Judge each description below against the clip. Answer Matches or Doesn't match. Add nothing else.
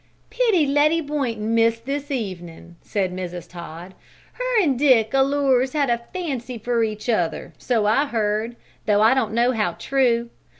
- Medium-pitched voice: Doesn't match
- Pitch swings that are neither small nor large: Matches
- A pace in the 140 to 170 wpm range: Matches